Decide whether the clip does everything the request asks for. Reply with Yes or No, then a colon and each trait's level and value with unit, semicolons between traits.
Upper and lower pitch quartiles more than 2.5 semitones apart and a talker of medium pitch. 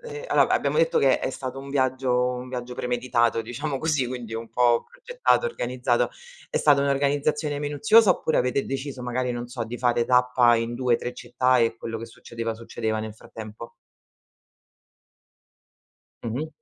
No: average, 2.9 semitones; low, 125 Hz